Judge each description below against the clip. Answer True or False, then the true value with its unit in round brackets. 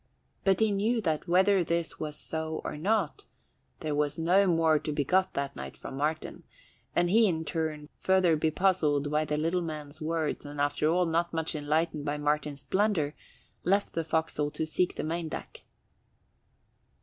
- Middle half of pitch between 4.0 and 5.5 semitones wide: False (3.0 semitones)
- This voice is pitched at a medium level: True (160 Hz)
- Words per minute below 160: False (175 wpm)